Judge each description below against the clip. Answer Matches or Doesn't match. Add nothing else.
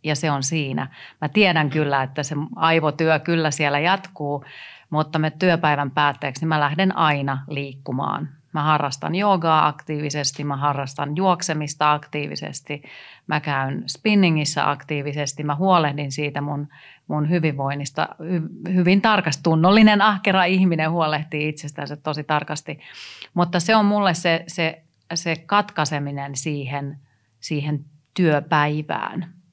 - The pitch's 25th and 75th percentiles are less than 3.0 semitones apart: Matches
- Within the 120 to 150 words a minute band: Matches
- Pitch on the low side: Doesn't match